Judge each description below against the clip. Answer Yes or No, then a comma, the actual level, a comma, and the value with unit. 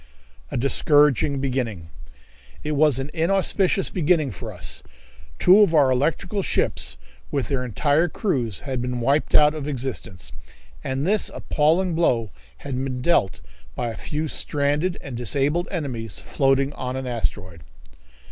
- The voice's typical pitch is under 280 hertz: Yes, medium, 140 Hz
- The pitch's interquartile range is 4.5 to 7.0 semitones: No, average, 3.9 semitones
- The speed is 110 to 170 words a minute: Yes, average, 140 wpm